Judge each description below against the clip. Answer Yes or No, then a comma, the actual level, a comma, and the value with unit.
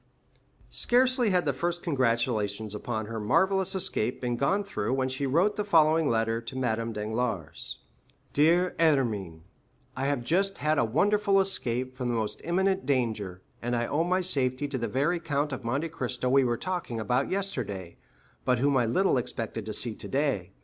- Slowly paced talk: No, average, 175 wpm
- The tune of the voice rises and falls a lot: Yes, wide, 6.6 semitones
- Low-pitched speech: Yes, low, 130 Hz